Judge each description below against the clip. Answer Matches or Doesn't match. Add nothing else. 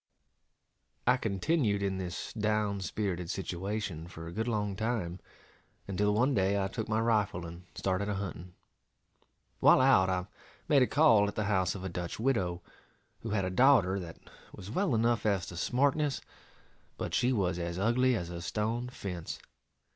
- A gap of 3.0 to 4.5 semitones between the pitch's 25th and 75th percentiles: Matches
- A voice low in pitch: Matches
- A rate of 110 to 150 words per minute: Doesn't match